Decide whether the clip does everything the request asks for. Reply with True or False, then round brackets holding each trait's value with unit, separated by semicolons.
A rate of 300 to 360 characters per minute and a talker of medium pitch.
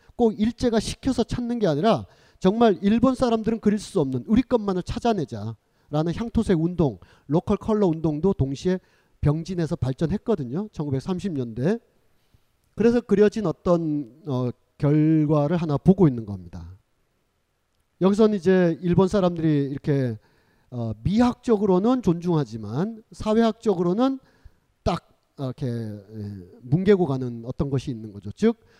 False (290 characters per minute; 170 Hz)